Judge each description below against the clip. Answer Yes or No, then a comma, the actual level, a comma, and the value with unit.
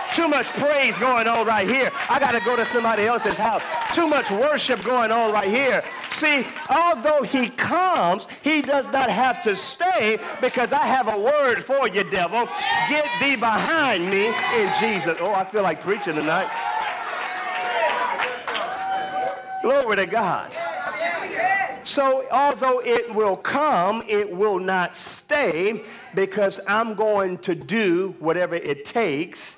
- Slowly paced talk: No, average, 145 wpm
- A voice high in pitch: Yes, high, 245 Hz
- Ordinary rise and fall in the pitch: No, wide, 6.0 semitones